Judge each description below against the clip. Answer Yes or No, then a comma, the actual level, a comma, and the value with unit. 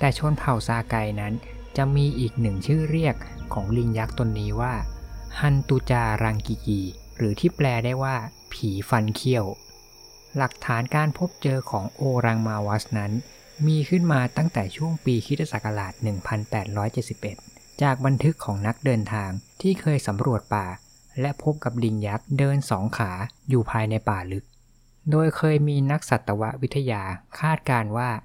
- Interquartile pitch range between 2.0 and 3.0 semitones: No, average, 4.5 semitones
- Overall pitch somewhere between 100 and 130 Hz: Yes, low, 120 Hz